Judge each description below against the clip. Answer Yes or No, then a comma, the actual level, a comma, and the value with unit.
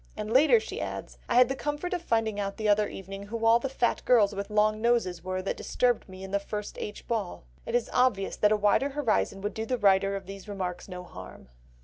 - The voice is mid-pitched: No, high, 210 Hz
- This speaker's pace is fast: Yes, fast, 240 wpm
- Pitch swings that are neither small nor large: Yes, average, 3.3 semitones